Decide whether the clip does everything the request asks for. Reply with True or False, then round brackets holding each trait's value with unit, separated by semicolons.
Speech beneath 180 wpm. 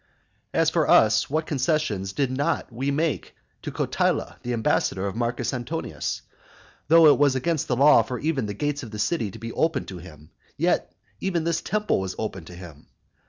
False (190 wpm)